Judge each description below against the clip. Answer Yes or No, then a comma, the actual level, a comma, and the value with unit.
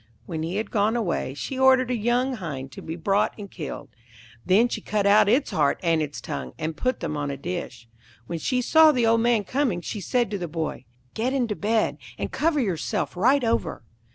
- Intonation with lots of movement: Yes, wide, 6.9 semitones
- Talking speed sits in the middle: No, fast, 210 wpm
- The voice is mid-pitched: No, high, 205 Hz